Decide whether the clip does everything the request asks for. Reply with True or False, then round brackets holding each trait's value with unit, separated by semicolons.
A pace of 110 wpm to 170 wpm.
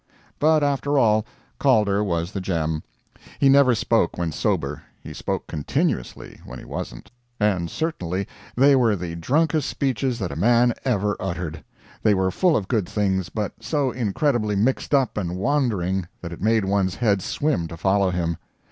True (165 wpm)